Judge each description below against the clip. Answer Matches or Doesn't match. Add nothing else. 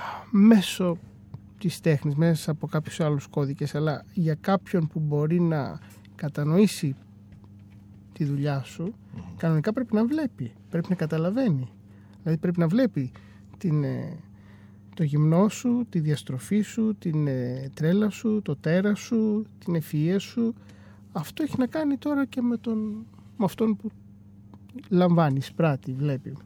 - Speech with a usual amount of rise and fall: Doesn't match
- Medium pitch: Matches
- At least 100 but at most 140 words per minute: Matches